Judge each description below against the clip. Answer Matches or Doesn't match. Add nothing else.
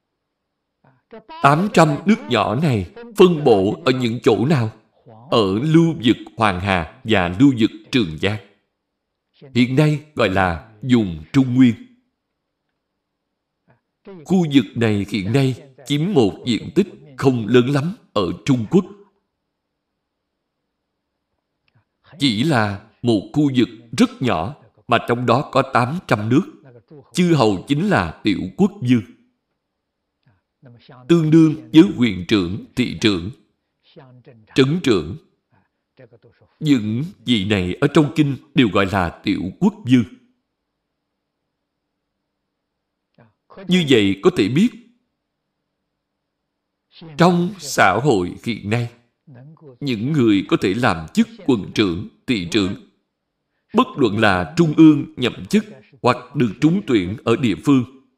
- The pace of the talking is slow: Matches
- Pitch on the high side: Doesn't match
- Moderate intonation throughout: Doesn't match